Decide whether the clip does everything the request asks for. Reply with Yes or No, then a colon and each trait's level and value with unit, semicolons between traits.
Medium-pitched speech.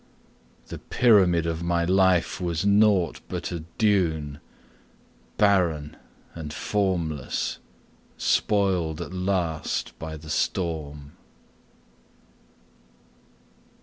No: very low, 85 Hz